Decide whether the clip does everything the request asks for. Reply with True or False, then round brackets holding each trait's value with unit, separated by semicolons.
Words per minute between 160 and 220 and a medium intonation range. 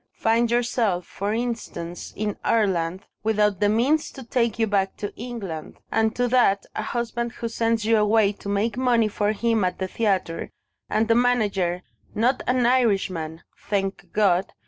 True (165 wpm; 3.2 semitones)